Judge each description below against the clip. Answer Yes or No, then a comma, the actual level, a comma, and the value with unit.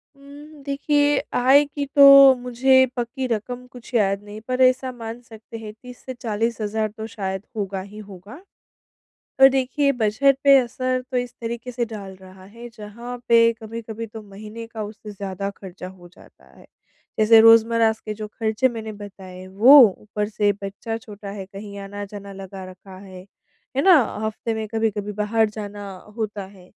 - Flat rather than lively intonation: No, average, 3.4 semitones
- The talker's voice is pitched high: Yes, high, 220 Hz